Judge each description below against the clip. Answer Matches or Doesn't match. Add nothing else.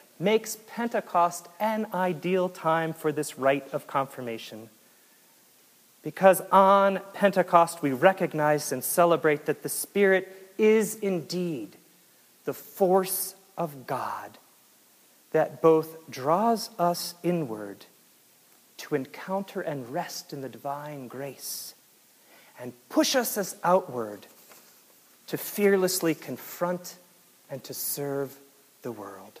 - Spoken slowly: Matches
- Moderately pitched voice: Matches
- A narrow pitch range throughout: Doesn't match